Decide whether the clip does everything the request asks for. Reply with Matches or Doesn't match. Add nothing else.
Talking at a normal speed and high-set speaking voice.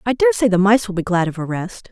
Doesn't match